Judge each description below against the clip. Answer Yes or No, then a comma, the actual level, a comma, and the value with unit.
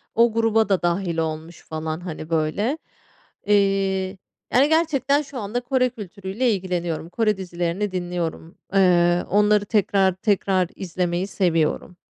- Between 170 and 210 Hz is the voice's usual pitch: Yes, high, 190 Hz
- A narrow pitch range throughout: No, average, 4.1 semitones